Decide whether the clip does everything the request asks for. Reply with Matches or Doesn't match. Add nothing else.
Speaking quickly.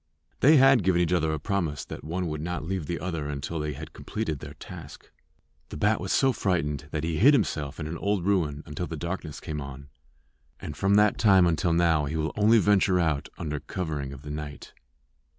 Matches